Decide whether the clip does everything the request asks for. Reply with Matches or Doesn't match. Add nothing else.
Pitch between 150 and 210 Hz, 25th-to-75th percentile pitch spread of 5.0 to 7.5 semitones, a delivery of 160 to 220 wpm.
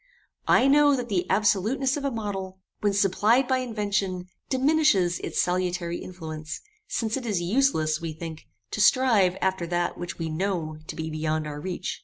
Matches